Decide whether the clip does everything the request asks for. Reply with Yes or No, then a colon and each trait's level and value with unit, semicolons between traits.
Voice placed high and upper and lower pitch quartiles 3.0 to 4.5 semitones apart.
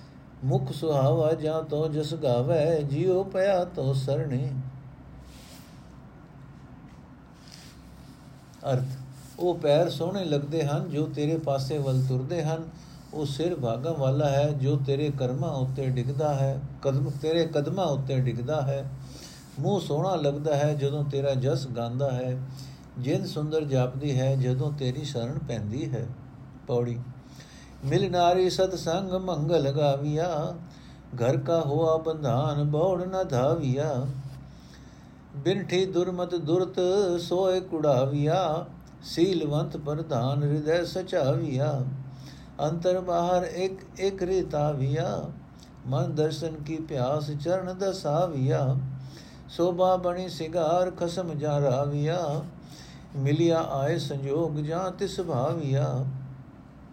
No: medium, 150 Hz; average, 3.7 semitones